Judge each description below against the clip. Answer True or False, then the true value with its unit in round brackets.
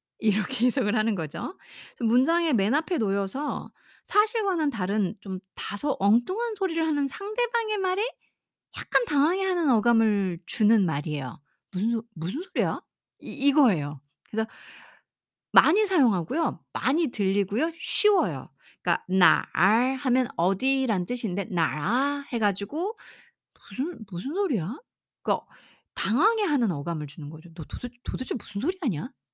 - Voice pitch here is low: False (235 Hz)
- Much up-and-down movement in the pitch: True (8.1 semitones)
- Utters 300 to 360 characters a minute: False (290 characters per minute)